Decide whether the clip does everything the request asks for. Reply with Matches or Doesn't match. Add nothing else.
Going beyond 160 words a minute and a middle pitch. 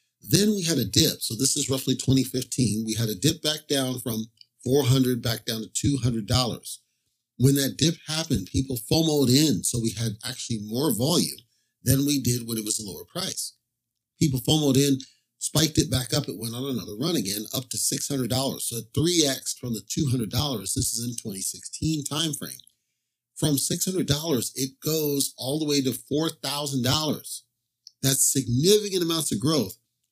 Doesn't match